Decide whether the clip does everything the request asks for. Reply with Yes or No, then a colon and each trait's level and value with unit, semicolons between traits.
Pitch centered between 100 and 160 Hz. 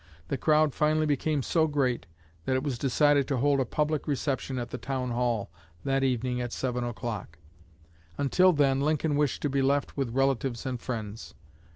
Yes: low, 135 Hz